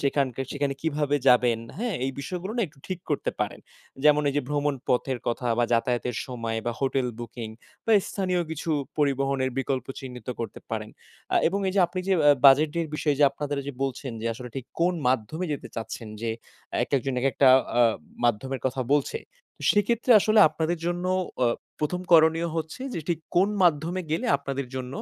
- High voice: No, medium, 140 Hz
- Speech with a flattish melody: No, average, 4.6 semitones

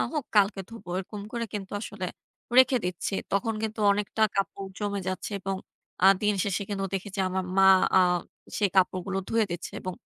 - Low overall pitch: No, high, 200 Hz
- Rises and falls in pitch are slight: Yes, narrow, 1.9 semitones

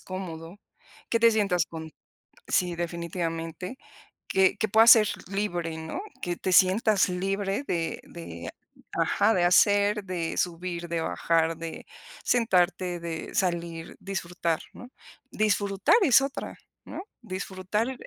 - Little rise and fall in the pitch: No, average, 3.2 semitones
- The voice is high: No, medium, 180 Hz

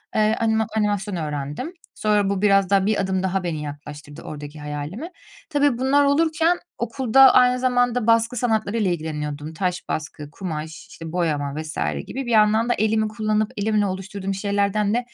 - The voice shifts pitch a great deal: Yes, wide, 6.0 semitones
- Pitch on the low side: No, high, 205 Hz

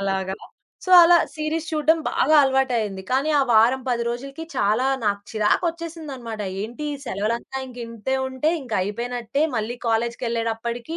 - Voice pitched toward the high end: Yes, high, 240 Hz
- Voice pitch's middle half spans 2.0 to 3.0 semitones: No, average, 3.8 semitones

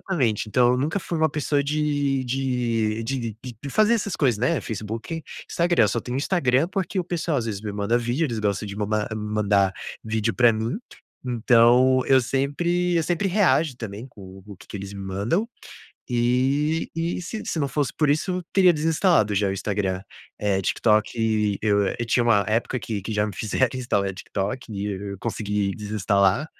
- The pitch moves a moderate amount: No, wide, 6.0 semitones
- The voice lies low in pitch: Yes, low, 120 Hz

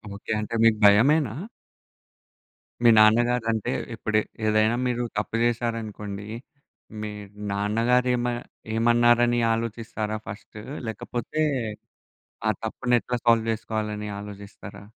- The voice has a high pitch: No, low, 115 Hz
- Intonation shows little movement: Yes, narrow, 1.9 semitones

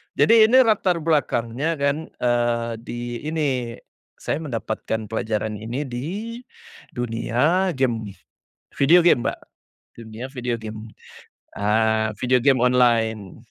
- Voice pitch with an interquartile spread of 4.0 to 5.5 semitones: Yes, average, 4.9 semitones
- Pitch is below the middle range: Yes, low, 120 Hz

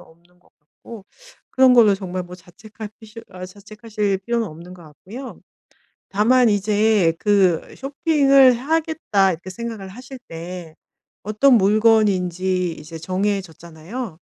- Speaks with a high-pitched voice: Yes, high, 200 Hz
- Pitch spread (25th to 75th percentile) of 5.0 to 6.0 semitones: No, average, 4.3 semitones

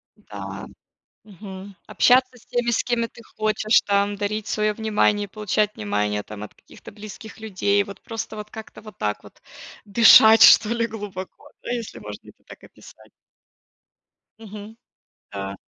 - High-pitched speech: Yes, high, 210 Hz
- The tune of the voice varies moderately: No, narrow, 1.8 semitones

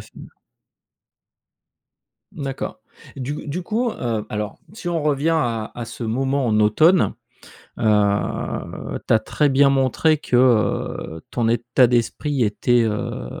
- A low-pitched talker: Yes, low, 125 Hz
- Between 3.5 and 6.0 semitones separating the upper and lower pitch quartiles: Yes, average, 4.8 semitones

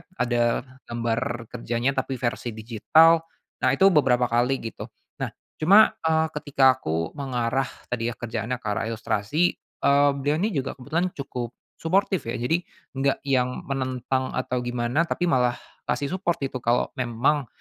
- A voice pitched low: Yes, low, 130 Hz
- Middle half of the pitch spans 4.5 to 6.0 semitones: No, average, 3.3 semitones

